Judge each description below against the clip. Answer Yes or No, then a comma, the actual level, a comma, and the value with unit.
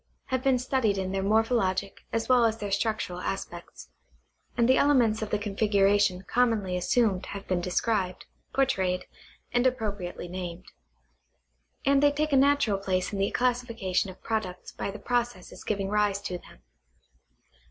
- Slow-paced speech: No, average, 150 wpm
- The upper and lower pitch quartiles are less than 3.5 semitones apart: No, average, 4.3 semitones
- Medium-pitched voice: No, high, 210 Hz